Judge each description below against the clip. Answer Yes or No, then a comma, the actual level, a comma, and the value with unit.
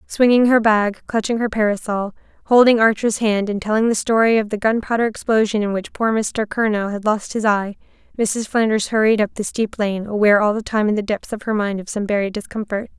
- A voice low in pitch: No, high, 215 Hz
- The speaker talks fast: Yes, fast, 215 wpm